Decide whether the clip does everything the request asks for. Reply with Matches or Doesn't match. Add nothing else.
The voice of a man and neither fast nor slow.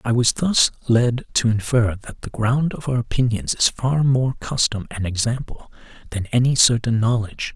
Matches